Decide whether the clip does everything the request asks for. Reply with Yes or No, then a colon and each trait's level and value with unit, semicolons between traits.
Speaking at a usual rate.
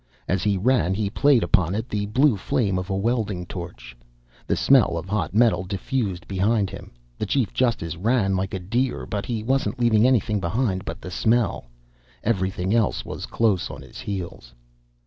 Yes: average, 180 wpm